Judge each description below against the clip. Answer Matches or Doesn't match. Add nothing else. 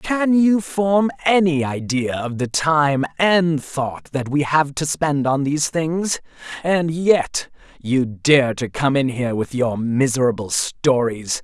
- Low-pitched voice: Doesn't match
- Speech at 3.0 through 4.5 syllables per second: Matches